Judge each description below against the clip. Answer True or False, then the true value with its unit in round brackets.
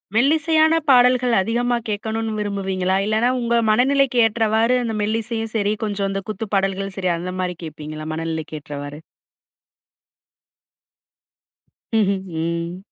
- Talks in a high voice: True (210 Hz)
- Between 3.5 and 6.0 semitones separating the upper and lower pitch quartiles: True (4.1 semitones)